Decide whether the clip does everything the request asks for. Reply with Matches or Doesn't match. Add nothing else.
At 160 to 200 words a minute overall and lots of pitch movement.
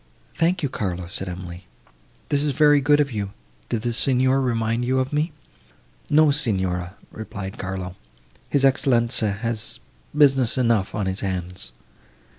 Doesn't match